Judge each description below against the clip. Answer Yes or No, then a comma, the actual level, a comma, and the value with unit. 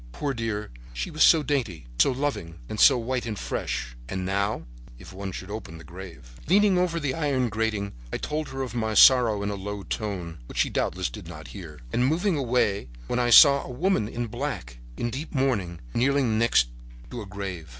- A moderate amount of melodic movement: No, wide, 6.2 semitones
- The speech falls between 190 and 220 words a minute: Yes, average, 200 wpm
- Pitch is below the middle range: Yes, low, 110 Hz